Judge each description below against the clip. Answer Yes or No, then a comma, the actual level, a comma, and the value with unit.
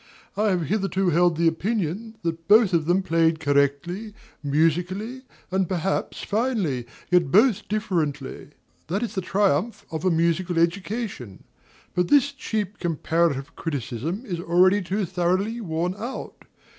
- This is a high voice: No, medium, 180 Hz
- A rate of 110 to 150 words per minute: Yes, average, 140 wpm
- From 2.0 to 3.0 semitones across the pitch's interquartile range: No, average, 4.0 semitones